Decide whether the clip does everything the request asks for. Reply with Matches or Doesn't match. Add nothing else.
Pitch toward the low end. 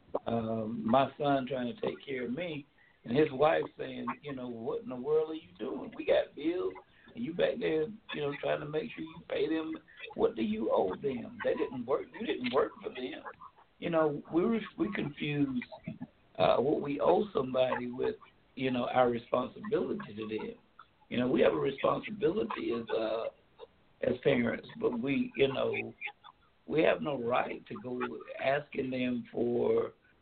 Doesn't match